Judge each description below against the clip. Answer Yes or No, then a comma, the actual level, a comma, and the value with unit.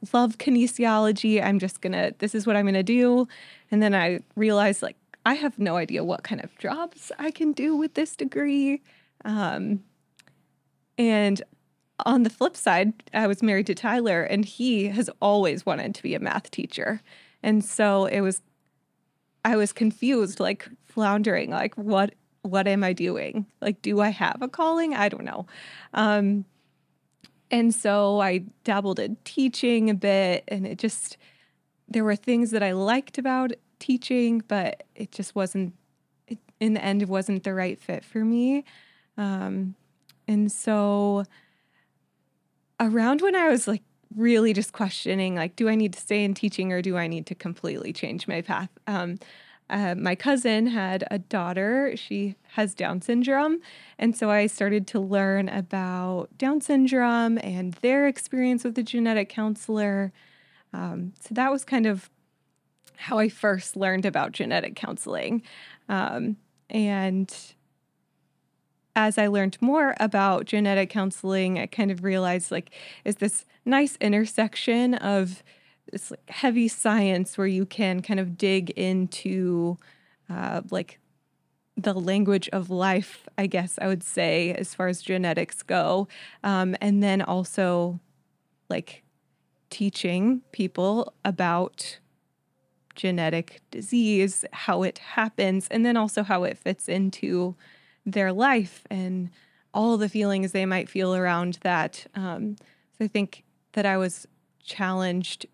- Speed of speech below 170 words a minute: Yes, average, 150 wpm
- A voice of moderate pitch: No, high, 205 Hz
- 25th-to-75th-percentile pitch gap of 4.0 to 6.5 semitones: No, average, 3.2 semitones